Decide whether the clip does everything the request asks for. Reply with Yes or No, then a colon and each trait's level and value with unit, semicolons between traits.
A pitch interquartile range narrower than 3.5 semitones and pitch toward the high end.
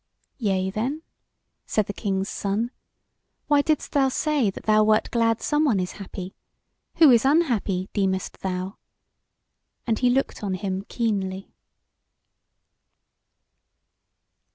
No: average, 5.0 semitones; high, 215 Hz